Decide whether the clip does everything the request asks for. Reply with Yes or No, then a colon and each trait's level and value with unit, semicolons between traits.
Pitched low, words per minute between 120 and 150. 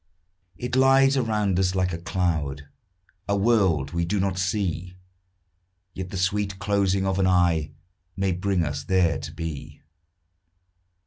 Yes: very low, 95 Hz; average, 140 wpm